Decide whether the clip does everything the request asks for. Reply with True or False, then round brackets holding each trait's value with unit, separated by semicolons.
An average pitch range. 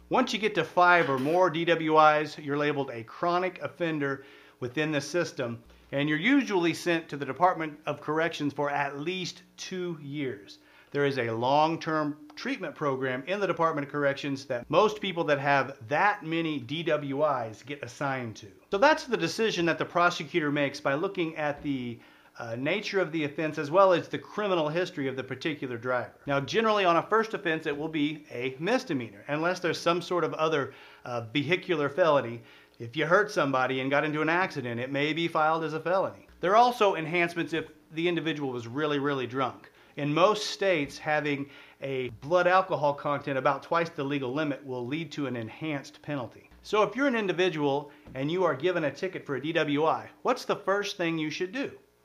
True (3.8 semitones)